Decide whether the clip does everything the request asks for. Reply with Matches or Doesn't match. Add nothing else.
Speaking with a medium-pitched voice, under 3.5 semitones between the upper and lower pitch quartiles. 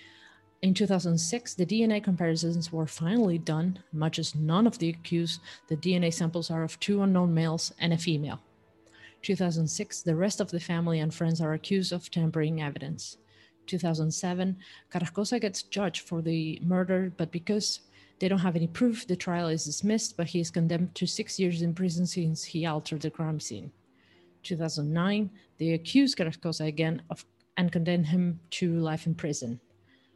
Matches